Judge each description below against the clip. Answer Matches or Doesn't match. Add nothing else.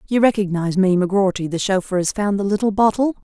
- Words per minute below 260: Matches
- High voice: Matches